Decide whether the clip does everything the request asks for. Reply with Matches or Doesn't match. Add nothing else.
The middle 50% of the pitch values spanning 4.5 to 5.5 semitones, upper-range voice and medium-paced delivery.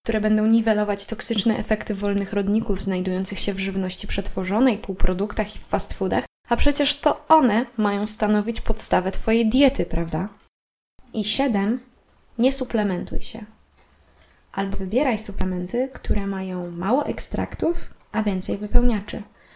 Doesn't match